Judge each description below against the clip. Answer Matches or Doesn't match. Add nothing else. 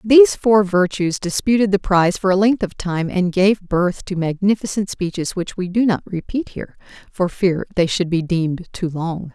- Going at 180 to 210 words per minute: Matches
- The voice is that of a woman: Matches